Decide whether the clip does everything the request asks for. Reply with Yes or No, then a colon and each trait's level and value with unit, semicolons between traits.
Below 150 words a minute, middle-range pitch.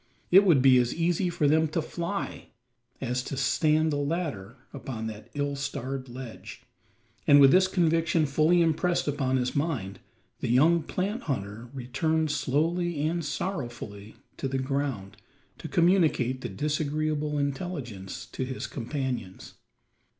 Yes: average, 140 wpm; medium, 145 Hz